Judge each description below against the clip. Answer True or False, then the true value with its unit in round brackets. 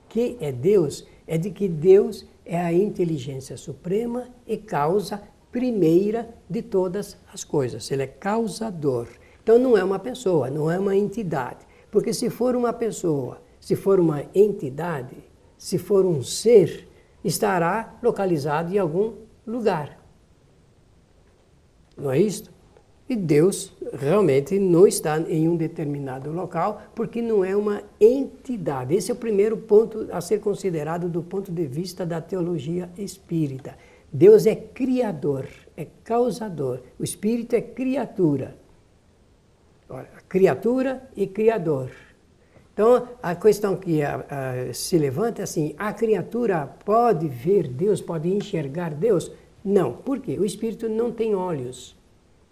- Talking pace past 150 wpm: False (135 wpm)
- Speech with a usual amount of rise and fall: False (5.8 semitones)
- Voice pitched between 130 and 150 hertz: False (190 Hz)